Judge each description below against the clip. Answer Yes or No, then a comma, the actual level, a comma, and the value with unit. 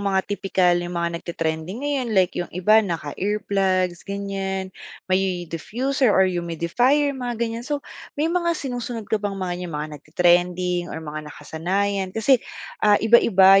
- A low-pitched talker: No, high, 195 Hz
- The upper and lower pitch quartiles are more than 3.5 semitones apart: Yes, average, 4.2 semitones